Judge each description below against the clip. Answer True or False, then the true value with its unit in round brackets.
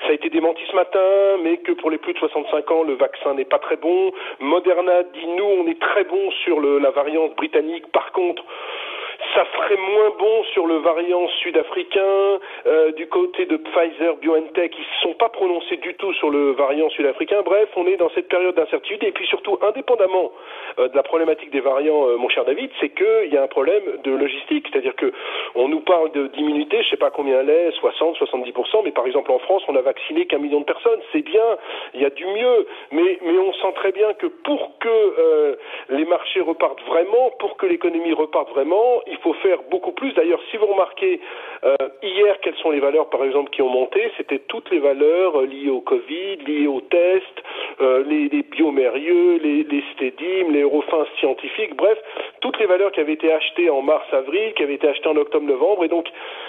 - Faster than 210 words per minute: True (220 wpm)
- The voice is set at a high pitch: True (335 Hz)